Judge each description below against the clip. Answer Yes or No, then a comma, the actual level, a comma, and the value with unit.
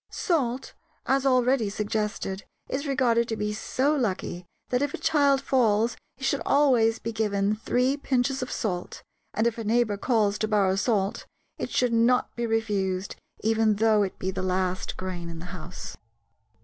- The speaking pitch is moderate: No, high, 225 Hz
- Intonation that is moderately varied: Yes, average, 4.0 semitones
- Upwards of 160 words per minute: Yes, average, 170 wpm